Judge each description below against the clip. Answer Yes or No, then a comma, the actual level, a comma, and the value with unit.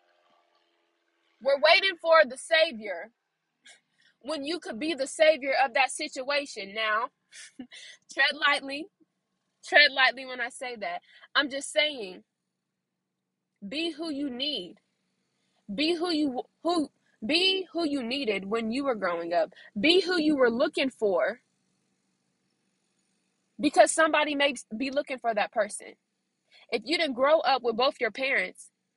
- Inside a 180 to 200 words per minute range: No, slow, 135 wpm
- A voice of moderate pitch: No, very high, 285 Hz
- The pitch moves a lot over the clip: No, average, 4.4 semitones